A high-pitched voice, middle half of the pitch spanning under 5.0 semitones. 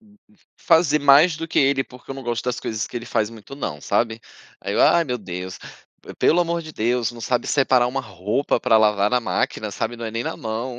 No: low, 120 Hz; average, 4.0 semitones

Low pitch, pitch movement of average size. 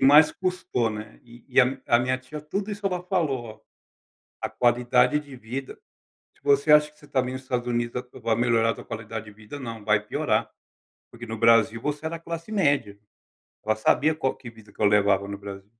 Yes: low, 125 Hz; average, 4.9 semitones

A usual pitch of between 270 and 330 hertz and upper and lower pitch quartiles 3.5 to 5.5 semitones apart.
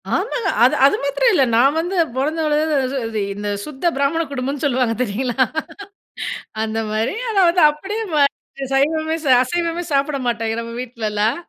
Yes: very high, 275 Hz; average, 4.8 semitones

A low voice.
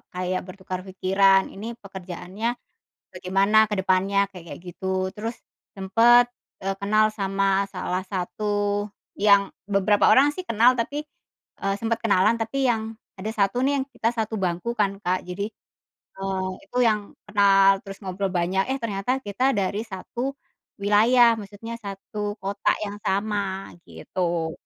No: high, 200 Hz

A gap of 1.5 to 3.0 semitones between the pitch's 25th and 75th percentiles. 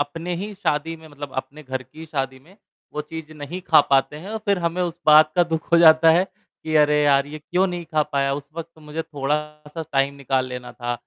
Yes: average, 2.7 semitones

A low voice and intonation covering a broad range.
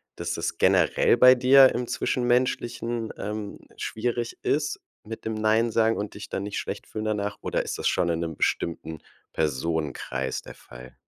Yes: low, 110 Hz; wide, 5.8 semitones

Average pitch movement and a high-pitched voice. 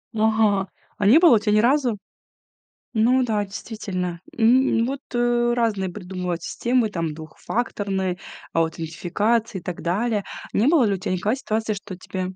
Yes: average, 4.3 semitones; high, 210 Hz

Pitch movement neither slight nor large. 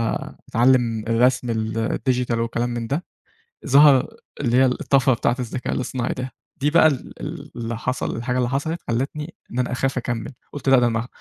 No: narrow, 2.3 semitones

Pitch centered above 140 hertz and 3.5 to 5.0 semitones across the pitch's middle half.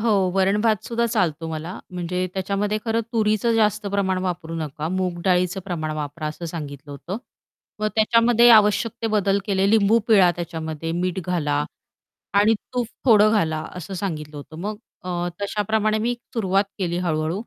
Yes: high, 190 Hz; average, 4.3 semitones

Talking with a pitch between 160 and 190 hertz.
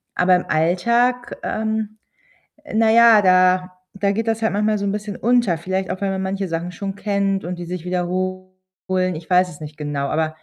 Yes: medium, 185 Hz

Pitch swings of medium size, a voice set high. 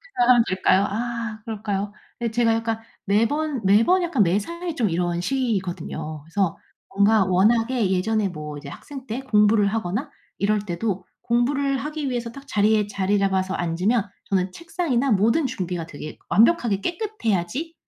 Yes: average, 4.8 semitones; high, 215 Hz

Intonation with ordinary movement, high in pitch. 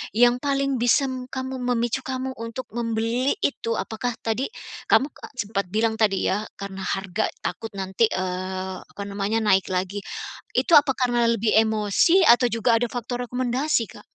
Yes: average, 3.5 semitones; high, 230 Hz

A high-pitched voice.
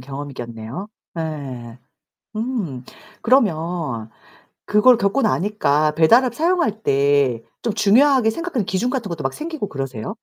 No: medium, 180 Hz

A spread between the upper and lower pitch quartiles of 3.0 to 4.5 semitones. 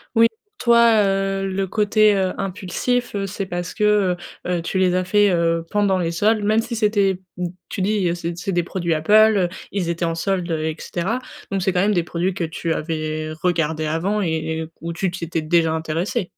Yes: average, 3.3 semitones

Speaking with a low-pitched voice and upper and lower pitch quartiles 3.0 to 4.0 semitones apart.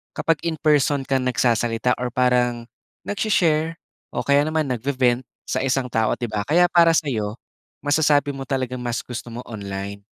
Yes: low, 130 Hz; average, 3.5 semitones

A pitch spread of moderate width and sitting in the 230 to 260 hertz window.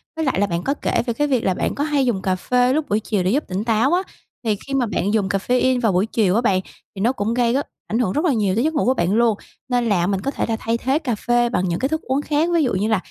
Yes: average, 4.8 semitones; high, 235 Hz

